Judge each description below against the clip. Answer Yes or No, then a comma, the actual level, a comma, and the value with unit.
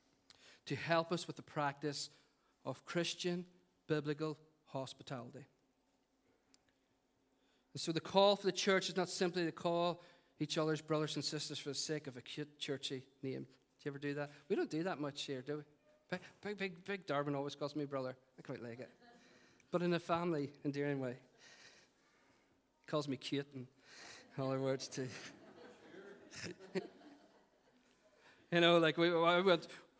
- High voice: No, medium, 150 Hz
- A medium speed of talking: Yes, average, 160 wpm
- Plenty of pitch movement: No, average, 3.7 semitones